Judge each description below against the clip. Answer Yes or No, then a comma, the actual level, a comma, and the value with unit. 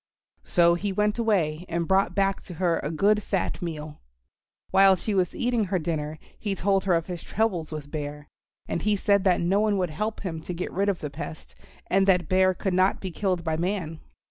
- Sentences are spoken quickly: Yes, fast, 215 wpm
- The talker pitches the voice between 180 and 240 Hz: Yes, medium, 185 Hz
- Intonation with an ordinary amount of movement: Yes, average, 3.1 semitones